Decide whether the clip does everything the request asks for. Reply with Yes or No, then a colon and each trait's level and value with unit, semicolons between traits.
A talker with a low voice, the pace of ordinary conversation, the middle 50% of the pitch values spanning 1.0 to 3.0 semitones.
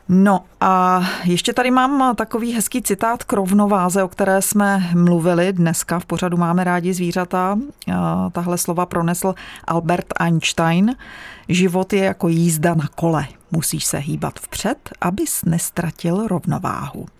No: medium, 185 Hz; average, 135 wpm; average, 2.7 semitones